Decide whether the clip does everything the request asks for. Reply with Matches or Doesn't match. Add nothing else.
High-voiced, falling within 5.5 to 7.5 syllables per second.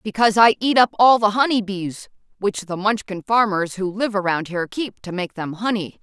Doesn't match